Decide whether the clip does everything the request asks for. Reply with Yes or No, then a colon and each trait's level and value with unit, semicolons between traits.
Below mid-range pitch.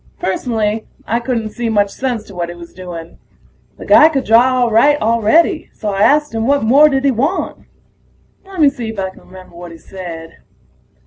No: high, 225 Hz